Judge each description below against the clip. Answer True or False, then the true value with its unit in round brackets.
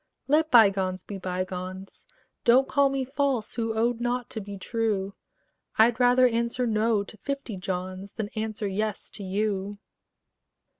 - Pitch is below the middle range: False (220 Hz)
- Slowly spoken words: False (145 wpm)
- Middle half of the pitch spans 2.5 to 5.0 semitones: True (3.8 semitones)